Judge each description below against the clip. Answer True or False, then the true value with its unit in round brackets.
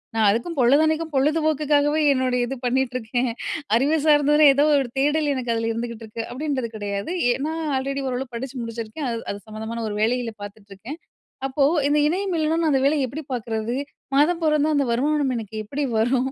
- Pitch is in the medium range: False (265 Hz)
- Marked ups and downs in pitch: False (4.3 semitones)